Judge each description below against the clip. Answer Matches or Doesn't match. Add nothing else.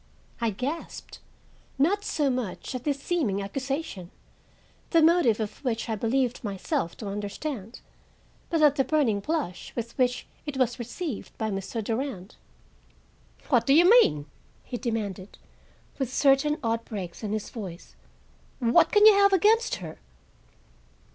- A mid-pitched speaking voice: Doesn't match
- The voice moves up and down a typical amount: Doesn't match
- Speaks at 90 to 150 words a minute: Matches